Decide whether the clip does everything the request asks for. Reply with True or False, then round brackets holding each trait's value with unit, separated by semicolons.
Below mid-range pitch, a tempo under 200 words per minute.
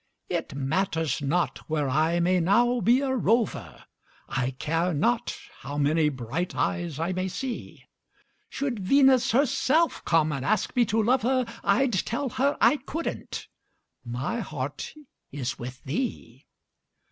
False (185 Hz; 140 wpm)